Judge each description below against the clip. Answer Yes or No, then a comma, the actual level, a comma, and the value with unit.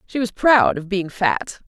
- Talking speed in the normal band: No, fast, 215 wpm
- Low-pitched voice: No, high, 210 Hz